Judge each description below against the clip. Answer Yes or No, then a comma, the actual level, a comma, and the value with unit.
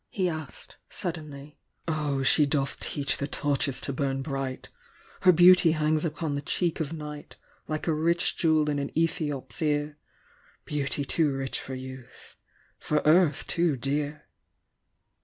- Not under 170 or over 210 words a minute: No, average, 145 wpm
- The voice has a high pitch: No, medium, 150 Hz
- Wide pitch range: No, narrow, 2.4 semitones